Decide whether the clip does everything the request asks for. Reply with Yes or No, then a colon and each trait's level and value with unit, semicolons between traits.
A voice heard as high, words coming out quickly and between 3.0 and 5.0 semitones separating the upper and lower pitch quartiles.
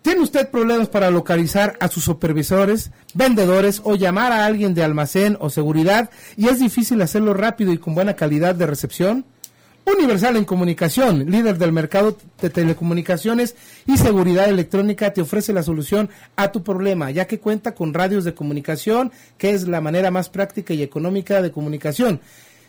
No: high, 195 Hz; average, 165 wpm; average, 3.8 semitones